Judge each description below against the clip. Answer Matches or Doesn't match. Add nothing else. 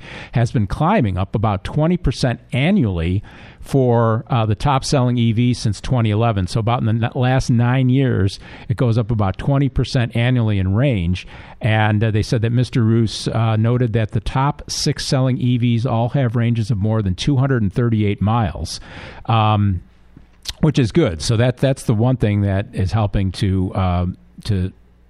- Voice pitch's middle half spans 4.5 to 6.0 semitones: Doesn't match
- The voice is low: Matches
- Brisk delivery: Doesn't match